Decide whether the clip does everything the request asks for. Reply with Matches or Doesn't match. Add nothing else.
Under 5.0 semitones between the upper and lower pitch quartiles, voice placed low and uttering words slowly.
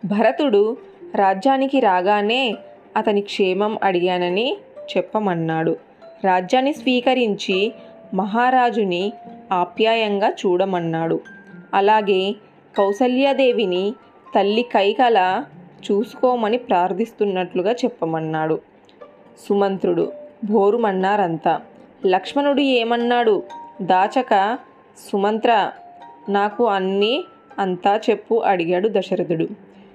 Doesn't match